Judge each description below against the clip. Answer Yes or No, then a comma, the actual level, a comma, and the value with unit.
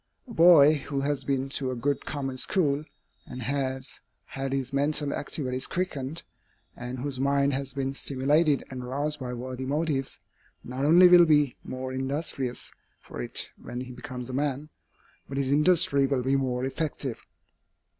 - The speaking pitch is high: No, low, 135 Hz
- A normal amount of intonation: No, narrow, 2.0 semitones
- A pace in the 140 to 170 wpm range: Yes, average, 160 wpm